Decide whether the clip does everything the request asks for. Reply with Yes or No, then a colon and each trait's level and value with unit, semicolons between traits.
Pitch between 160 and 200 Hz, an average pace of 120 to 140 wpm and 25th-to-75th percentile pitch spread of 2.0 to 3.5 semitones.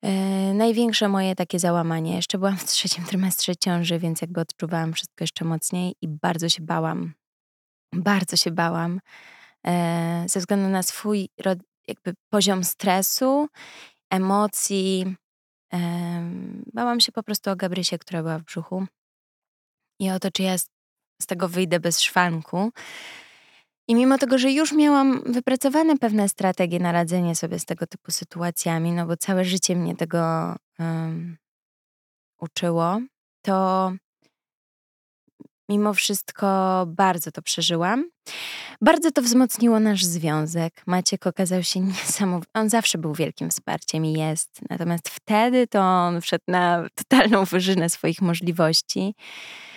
Yes: medium, 185 Hz; average, 135 wpm; average, 3.1 semitones